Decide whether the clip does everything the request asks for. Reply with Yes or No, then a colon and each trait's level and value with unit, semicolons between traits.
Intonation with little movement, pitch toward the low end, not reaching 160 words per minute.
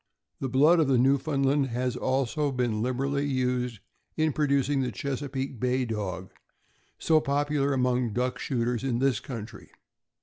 Yes: narrow, 2.2 semitones; low, 130 Hz; average, 140 wpm